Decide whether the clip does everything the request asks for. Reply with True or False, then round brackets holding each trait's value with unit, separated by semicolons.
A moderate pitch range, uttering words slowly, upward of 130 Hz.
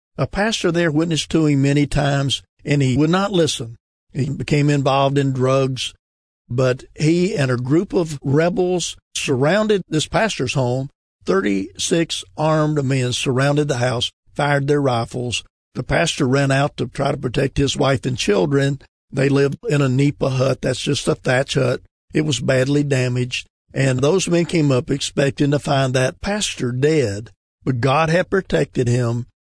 False (3.2 semitones; 165 wpm; 140 Hz)